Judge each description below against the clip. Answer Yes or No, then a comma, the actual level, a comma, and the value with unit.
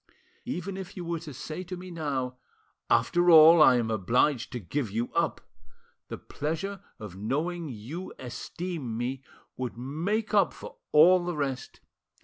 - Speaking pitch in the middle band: Yes, medium, 150 Hz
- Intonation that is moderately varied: No, wide, 5.9 semitones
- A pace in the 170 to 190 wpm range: No, average, 155 wpm